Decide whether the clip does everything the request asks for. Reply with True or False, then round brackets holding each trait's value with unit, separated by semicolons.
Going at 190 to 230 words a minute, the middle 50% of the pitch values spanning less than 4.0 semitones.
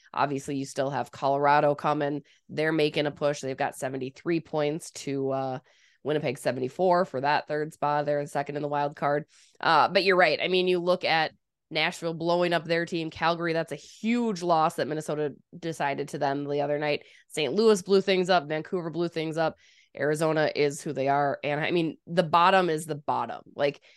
True (200 wpm; 2.9 semitones)